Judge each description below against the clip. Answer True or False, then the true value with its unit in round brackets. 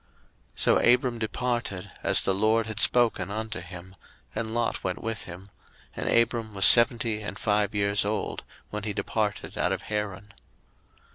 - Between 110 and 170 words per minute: True (160 wpm)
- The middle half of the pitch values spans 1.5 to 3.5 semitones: True (2.4 semitones)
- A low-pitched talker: True (105 Hz)